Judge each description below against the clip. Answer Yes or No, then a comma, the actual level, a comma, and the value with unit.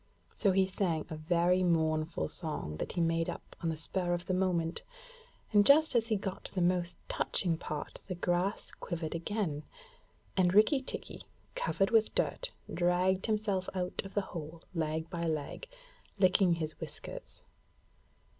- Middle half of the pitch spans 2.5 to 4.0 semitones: Yes, average, 2.8 semitones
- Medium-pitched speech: Yes, medium, 180 Hz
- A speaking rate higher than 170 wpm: No, average, 160 wpm